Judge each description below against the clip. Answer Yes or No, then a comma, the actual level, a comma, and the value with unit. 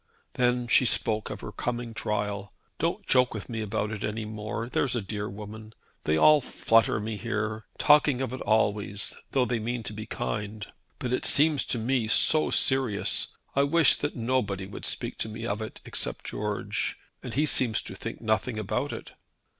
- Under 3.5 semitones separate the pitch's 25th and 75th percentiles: Yes, average, 3.0 semitones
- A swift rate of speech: No, average, 185 wpm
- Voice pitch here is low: Yes, low, 110 Hz